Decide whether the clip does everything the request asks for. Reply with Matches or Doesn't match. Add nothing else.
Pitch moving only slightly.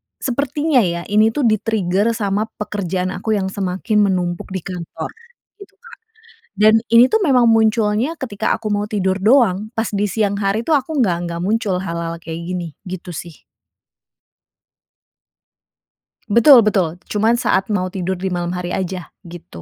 Doesn't match